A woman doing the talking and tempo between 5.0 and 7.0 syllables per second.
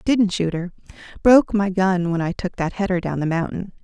Yes: female; 5.4 syllables/s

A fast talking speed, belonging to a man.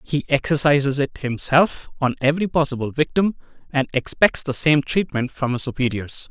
No: average, 150 wpm; male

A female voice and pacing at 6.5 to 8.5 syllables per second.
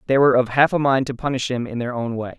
No: male; 6.8 syllables/s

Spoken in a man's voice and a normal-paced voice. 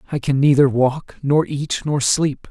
Yes: male; average, 190 wpm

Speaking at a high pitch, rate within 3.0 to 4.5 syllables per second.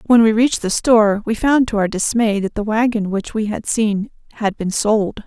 No: high, 215 Hz; 5.0 syllables/s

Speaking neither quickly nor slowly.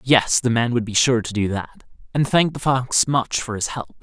No: fast, 255 wpm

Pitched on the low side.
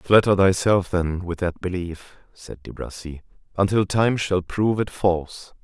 Yes: very low, 95 Hz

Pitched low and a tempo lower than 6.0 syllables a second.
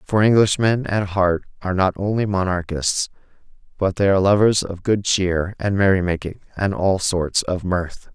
Yes: very low, 95 Hz; 4.7 syllables/s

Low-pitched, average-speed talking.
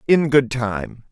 Yes: low, 125 Hz; average, 160 wpm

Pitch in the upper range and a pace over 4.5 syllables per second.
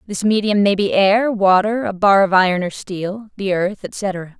No: high, 200 Hz; 4.3 syllables/s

